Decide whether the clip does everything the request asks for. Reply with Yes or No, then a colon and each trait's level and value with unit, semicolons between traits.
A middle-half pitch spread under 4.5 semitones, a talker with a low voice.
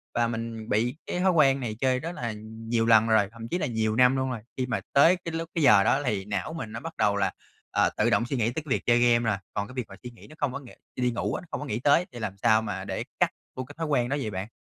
Yes: average, 3.7 semitones; low, 120 Hz